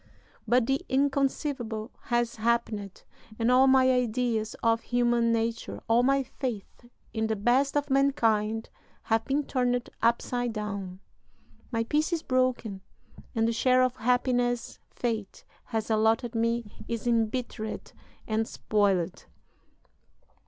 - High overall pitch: Yes, high, 235 Hz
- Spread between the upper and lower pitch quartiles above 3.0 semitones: No, narrow, 2.4 semitones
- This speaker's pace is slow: Yes, slow, 125 wpm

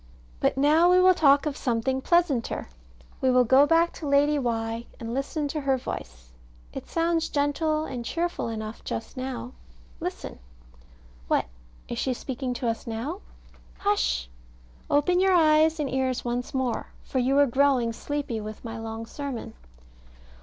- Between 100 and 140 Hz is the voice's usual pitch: No, very high, 270 Hz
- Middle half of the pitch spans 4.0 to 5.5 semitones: Yes, average, 4.6 semitones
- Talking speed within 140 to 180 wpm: Yes, average, 155 wpm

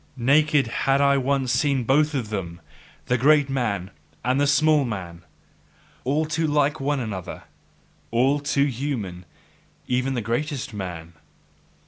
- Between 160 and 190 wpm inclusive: No, slow, 135 wpm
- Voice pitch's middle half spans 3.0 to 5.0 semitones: Yes, average, 4.3 semitones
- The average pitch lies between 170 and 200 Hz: No, low, 135 Hz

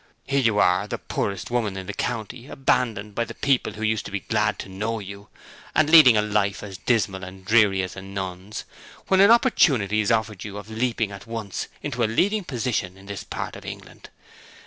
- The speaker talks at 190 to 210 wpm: Yes, fast, 205 wpm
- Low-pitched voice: Yes, low, 105 Hz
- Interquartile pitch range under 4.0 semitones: Yes, average, 3.4 semitones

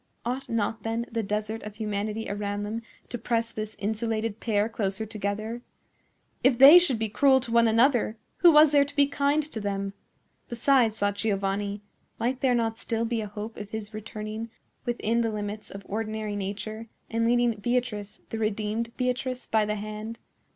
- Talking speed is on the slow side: No, average, 175 wpm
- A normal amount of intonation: No, narrow, 2.3 semitones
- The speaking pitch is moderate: No, high, 220 Hz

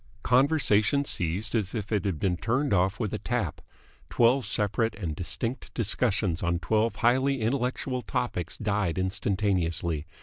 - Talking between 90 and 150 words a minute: Yes, average, 140 wpm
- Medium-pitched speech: No, low, 105 Hz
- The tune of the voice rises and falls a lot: No, average, 4.9 semitones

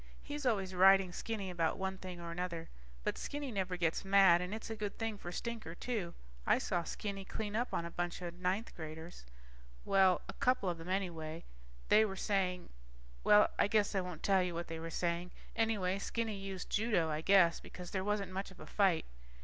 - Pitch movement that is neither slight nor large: Yes, average, 3.0 semitones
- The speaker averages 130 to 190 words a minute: No, fast, 205 wpm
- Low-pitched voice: No, high, 190 Hz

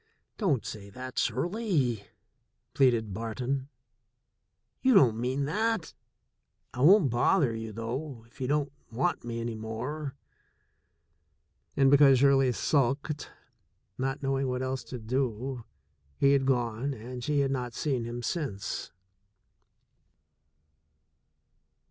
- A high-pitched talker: No, low, 130 Hz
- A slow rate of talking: Yes, slow, 115 wpm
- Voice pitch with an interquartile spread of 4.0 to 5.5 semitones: No, average, 3.2 semitones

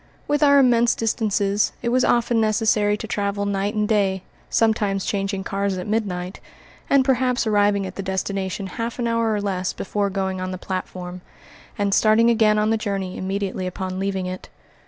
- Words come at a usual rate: Yes, average, 180 wpm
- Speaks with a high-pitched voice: Yes, high, 205 Hz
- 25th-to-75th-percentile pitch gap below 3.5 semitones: Yes, average, 2.7 semitones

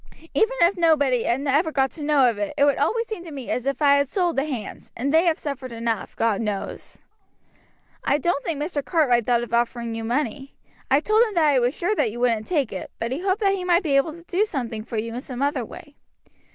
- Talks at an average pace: No, fast, 245 wpm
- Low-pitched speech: No, very high, 280 Hz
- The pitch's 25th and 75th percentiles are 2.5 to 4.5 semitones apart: No, wide, 5.5 semitones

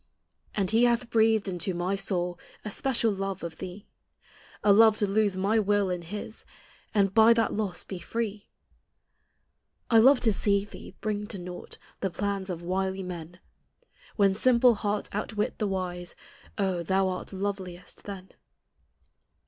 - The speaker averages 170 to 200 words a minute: No, average, 155 wpm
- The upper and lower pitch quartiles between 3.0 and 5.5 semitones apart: No, narrow, 2.6 semitones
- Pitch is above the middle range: Yes, high, 200 Hz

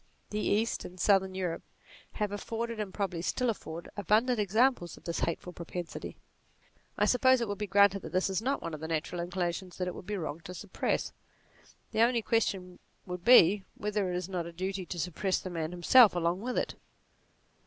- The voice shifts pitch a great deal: No, average, 3.2 semitones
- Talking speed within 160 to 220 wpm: Yes, average, 200 wpm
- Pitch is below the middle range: No, high, 190 Hz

